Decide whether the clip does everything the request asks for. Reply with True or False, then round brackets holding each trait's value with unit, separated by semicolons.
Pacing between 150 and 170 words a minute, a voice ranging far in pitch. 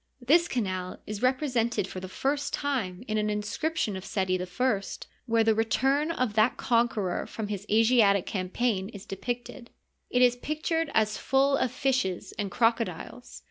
False (160 wpm; 4.3 semitones)